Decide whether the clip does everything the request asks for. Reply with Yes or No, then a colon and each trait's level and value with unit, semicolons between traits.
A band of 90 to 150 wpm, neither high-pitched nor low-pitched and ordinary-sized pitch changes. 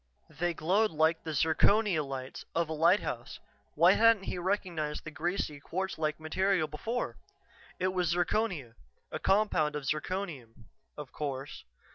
Yes: average, 140 wpm; medium, 165 Hz; average, 3.9 semitones